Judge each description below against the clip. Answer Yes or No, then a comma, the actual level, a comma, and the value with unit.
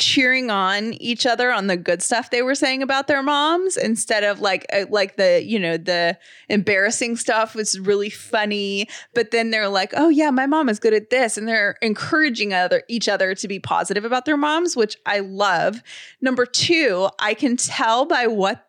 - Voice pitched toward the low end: No, high, 225 Hz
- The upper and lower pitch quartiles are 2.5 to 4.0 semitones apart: No, average, 4.4 semitones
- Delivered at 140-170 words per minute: No, average, 195 wpm